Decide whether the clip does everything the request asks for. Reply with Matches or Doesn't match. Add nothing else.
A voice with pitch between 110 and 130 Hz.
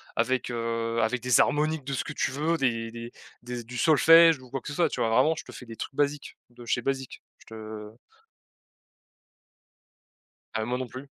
Matches